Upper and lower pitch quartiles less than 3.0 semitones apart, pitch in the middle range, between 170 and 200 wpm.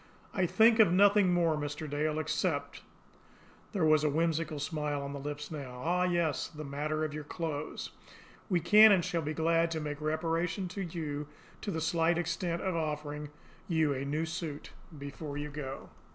Yes: narrow, 2.6 semitones; medium, 155 Hz; average, 180 wpm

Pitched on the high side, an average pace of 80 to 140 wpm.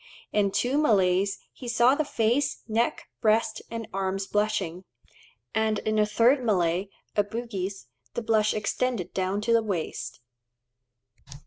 Yes: high, 215 Hz; slow, 135 wpm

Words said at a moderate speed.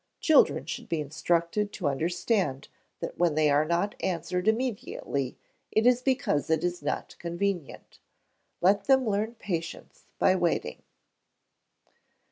No: slow, 125 wpm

